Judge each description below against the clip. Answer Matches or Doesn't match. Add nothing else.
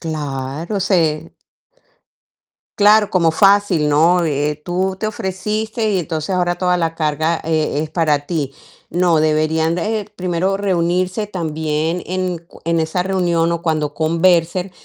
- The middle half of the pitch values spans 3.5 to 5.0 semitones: Doesn't match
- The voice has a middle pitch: Matches